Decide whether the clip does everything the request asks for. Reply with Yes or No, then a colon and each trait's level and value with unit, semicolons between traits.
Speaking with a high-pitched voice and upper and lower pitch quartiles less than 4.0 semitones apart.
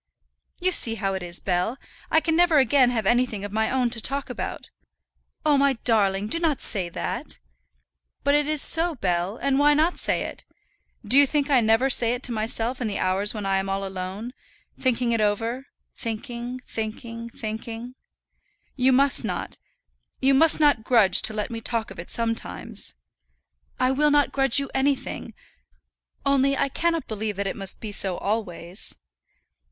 No: high, 235 Hz; average, 4.8 semitones